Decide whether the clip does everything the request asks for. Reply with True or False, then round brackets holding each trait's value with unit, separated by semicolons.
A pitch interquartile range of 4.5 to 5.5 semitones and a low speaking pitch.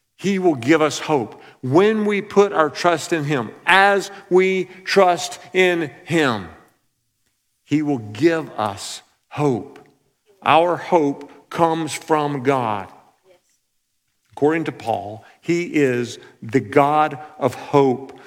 False (4.8 semitones; 150 Hz)